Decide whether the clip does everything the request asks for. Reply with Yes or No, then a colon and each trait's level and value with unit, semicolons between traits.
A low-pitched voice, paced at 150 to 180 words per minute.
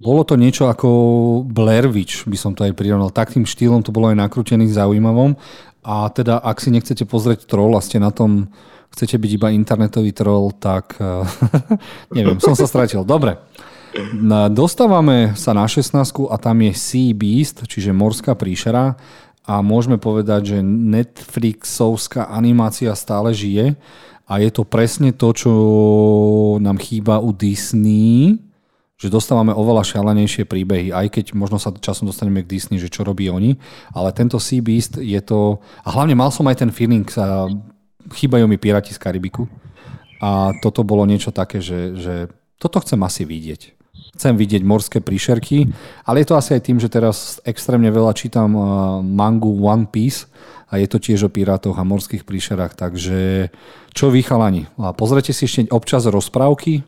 Yes: low, 110 Hz; average, 160 wpm